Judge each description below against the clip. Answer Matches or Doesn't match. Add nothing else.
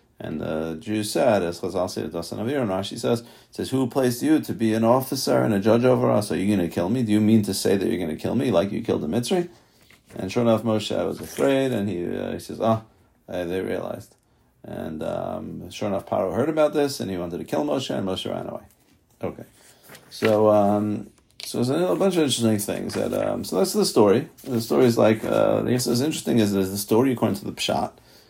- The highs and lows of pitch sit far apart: Doesn't match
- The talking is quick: Matches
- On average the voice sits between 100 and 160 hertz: Matches